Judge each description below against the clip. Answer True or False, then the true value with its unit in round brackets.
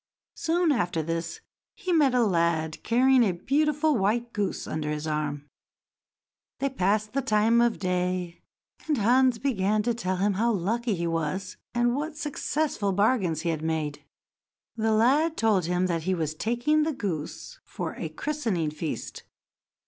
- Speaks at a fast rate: False (155 wpm)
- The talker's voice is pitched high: True (210 Hz)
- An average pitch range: False (7.1 semitones)